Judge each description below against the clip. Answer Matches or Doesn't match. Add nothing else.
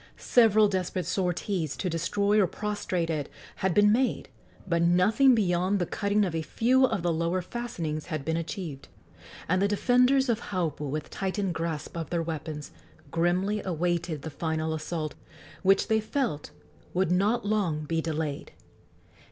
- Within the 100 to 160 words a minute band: Matches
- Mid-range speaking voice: Matches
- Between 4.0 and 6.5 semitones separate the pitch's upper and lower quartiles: Matches